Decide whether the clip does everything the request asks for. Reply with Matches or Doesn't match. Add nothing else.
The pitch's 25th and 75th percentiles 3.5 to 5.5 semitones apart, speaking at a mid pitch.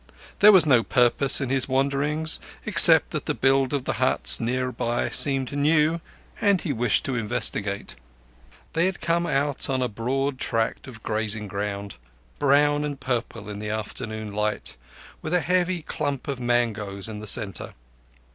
Doesn't match